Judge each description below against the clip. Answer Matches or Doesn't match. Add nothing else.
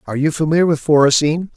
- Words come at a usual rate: Matches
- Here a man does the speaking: Matches